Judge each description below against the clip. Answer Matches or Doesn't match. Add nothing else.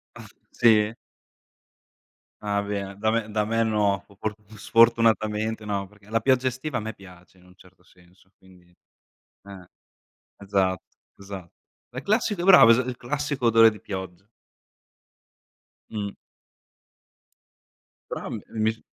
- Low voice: Matches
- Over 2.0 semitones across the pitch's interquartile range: Matches